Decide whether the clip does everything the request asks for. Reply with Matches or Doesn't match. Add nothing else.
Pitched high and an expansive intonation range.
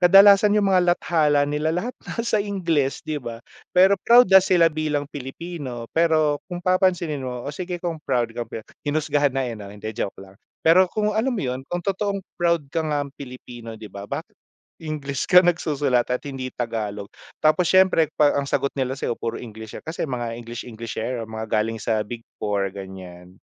Doesn't match